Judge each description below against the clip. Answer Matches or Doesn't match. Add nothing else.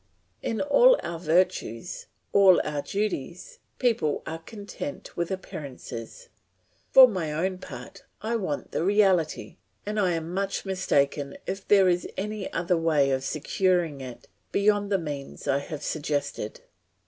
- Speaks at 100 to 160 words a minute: Matches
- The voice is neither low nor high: Matches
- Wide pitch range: Doesn't match